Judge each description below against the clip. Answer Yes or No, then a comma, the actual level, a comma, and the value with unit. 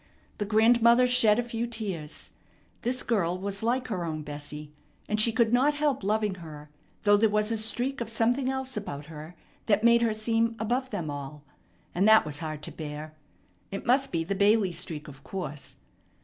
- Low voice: No, high, 210 Hz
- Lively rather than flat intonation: Yes, wide, 6.6 semitones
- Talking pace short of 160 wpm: No, average, 190 wpm